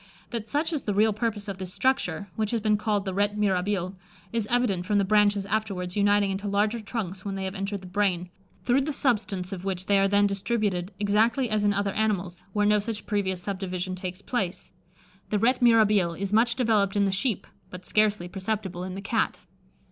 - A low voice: No, high, 205 Hz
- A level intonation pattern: Yes, narrow, 2.1 semitones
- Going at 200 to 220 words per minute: Yes, fast, 205 wpm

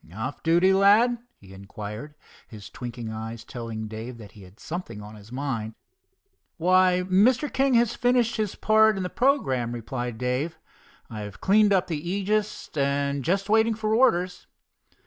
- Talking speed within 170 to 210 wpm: No, average, 155 wpm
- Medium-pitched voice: Yes, medium, 160 Hz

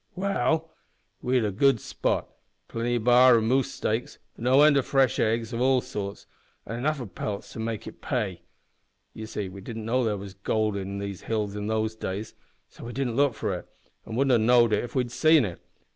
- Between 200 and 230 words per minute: Yes, fast, 205 wpm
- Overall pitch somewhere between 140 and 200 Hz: No, low, 115 Hz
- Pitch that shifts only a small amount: No, average, 3.3 semitones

